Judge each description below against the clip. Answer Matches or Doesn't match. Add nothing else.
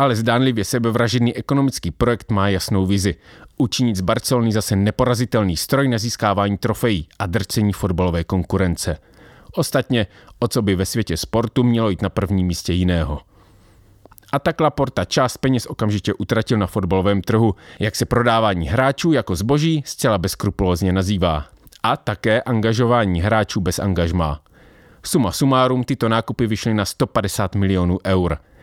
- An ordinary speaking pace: Matches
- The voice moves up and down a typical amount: Matches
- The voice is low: Matches